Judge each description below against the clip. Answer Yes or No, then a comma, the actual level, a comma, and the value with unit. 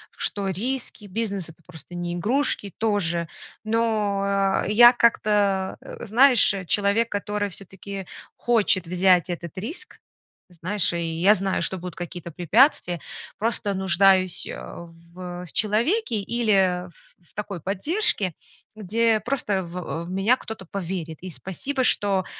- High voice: Yes, high, 195 Hz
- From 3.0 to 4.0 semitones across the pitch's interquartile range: Yes, average, 3.4 semitones